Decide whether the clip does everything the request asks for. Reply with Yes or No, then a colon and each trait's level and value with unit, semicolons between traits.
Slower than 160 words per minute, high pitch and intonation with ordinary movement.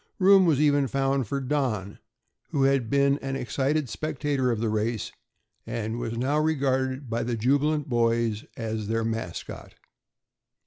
No: average, 145 wpm; low, 130 Hz; average, 3.7 semitones